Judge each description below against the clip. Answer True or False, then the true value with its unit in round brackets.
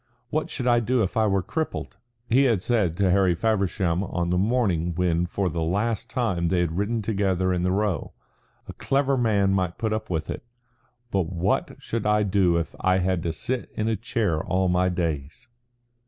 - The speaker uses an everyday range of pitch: True (4.0 semitones)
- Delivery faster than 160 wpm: True (200 wpm)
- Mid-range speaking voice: False (95 Hz)